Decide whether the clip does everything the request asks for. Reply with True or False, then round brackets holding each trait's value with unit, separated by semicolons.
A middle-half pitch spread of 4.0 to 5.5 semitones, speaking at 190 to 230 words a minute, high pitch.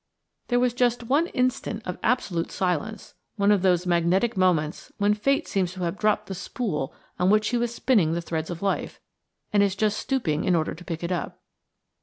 True (5.0 semitones; 205 wpm; 195 Hz)